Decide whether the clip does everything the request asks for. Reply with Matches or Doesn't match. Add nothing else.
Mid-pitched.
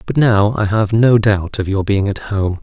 Doesn't match